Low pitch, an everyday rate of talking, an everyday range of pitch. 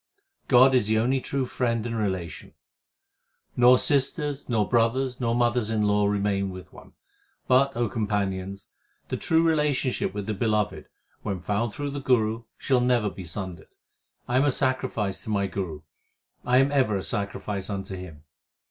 Yes: low, 110 Hz; average, 165 wpm; average, 4.4 semitones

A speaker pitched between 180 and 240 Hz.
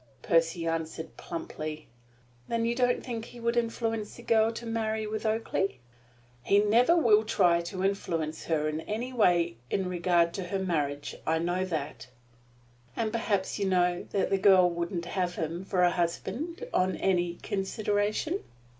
Yes: high, 190 Hz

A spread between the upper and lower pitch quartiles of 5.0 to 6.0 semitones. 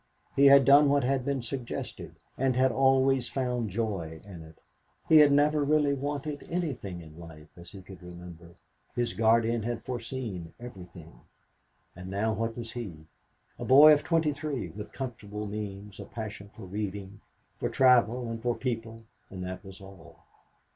Yes: wide, 5.6 semitones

